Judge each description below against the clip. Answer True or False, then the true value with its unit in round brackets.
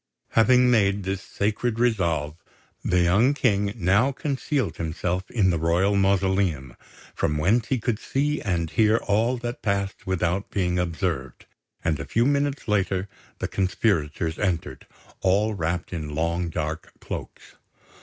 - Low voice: True (95 Hz)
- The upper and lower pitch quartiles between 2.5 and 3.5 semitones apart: False (4.8 semitones)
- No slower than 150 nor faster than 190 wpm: False (140 wpm)